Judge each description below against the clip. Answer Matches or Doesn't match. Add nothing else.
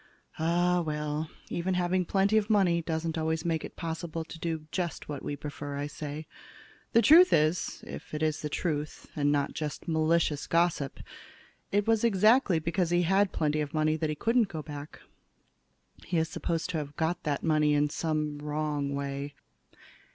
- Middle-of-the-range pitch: Matches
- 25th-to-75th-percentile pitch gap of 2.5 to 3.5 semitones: Matches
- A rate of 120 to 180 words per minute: Matches